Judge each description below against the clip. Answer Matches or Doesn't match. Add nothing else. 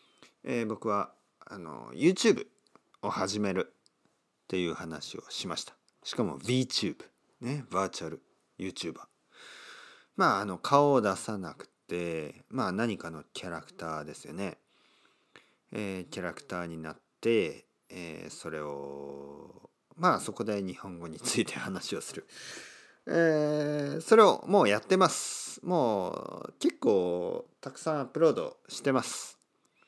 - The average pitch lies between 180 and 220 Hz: Doesn't match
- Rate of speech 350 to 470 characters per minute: Doesn't match